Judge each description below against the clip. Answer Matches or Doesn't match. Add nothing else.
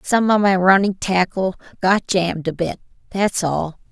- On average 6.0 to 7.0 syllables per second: Doesn't match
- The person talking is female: Matches